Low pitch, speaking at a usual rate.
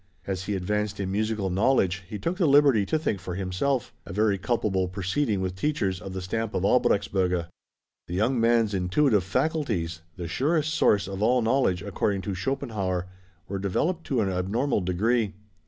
Yes: low, 100 Hz; average, 170 wpm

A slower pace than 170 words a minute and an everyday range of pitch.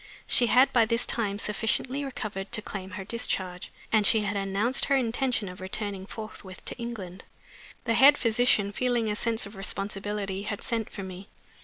No: average, 175 wpm; average, 3.0 semitones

